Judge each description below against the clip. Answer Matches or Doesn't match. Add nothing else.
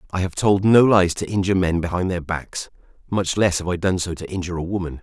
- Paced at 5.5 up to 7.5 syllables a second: Matches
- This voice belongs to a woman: Doesn't match